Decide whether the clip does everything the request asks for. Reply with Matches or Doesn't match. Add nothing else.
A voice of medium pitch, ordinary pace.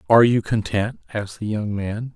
Doesn't match